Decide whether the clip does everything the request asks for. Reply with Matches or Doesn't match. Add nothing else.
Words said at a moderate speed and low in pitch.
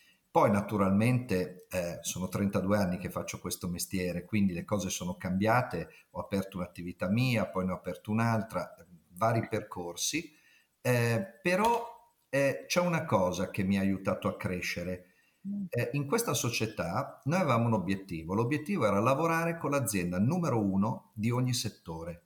Matches